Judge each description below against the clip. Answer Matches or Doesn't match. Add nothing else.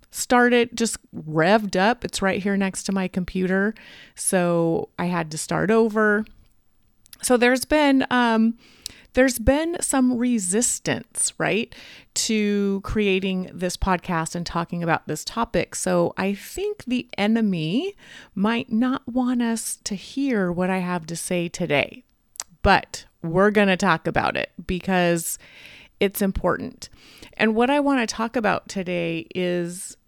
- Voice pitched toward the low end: Doesn't match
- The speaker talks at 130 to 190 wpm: Matches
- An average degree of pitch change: Matches